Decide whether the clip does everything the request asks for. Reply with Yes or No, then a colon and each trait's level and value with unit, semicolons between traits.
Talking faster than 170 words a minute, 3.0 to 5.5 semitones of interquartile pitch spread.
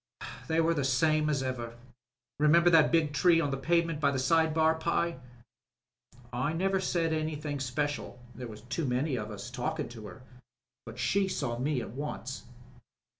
Yes: average, 180 wpm; average, 4.3 semitones